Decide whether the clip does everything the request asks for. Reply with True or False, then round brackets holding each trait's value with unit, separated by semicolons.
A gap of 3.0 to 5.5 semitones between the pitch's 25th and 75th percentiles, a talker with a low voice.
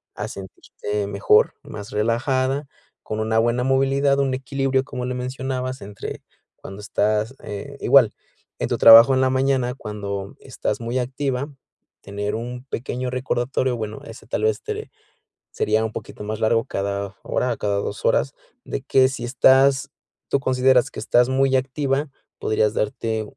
True (3.6 semitones; 125 Hz)